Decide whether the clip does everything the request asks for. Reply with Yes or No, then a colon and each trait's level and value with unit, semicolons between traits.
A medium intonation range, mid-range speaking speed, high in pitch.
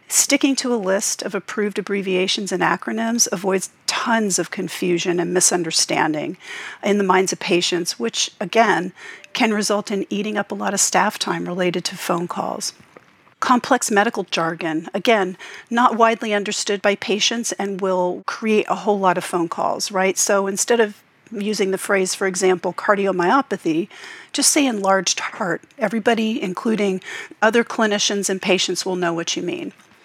Yes: average, 3.5 semitones; average, 160 wpm; high, 200 Hz